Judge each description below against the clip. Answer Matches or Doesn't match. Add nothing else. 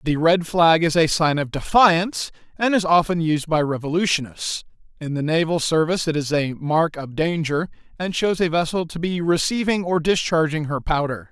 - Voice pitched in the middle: Matches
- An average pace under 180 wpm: Doesn't match